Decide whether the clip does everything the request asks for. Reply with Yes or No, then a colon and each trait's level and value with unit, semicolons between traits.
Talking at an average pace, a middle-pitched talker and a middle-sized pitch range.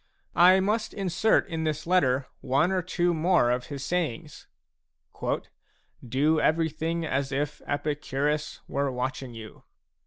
No: slow, 130 wpm; medium, 150 Hz; average, 4.0 semitones